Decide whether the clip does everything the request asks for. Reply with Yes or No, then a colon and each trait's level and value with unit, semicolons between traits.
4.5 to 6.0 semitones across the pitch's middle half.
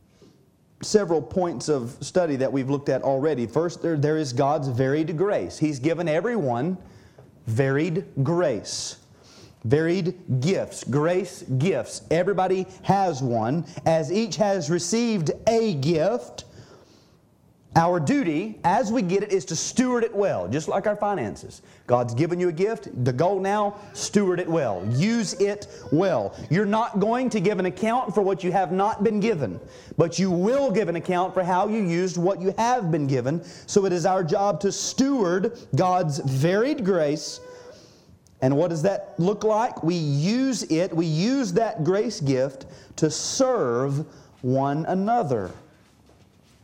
Yes: wide, 5.4 semitones